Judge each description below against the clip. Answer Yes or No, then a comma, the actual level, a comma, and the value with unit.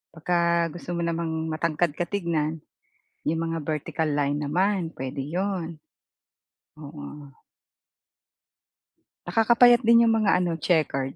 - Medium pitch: Yes, medium, 170 Hz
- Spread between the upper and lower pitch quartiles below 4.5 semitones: Yes, average, 3.9 semitones